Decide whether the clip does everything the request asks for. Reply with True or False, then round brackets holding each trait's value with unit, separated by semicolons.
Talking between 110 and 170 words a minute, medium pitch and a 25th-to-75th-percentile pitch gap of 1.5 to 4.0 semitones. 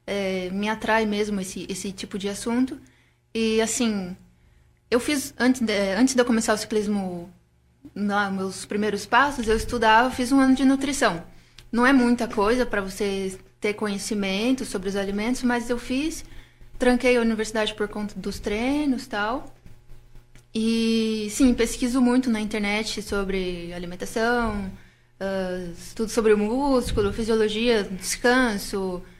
False (140 wpm; 220 Hz; 3.4 semitones)